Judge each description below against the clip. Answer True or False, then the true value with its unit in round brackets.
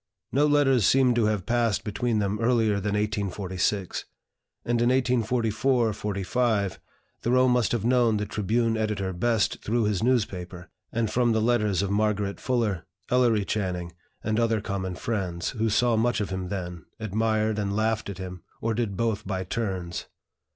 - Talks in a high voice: False (110 Hz)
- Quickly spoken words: False (160 wpm)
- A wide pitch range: False (3.1 semitones)